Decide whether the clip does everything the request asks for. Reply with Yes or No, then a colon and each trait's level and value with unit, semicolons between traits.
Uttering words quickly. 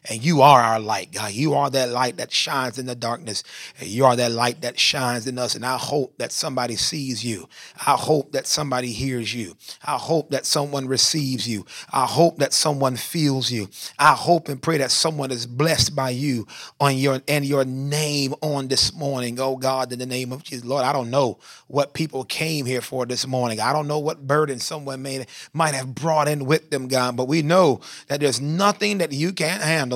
Yes: fast, 215 wpm